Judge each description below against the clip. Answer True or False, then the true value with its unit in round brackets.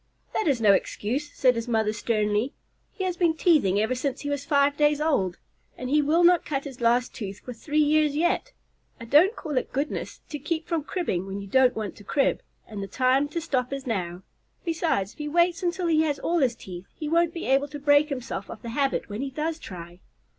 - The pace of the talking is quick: True (225 wpm)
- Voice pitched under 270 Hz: False (280 Hz)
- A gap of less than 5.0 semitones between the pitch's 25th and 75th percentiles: False (5.4 semitones)